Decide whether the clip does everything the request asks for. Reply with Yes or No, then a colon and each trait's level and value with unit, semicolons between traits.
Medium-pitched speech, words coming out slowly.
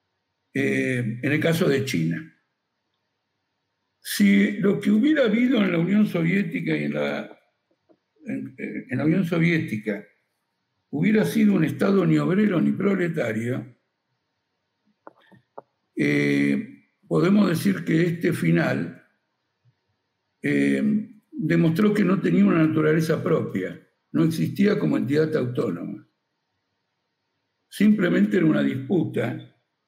Yes: medium, 160 Hz; slow, 110 wpm